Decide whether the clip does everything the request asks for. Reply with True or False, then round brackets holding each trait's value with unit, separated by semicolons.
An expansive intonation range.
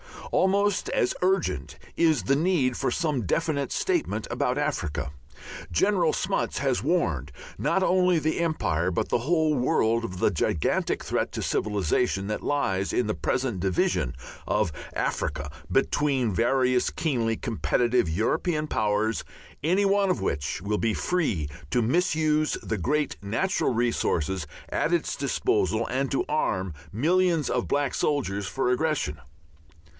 True (7.4 semitones)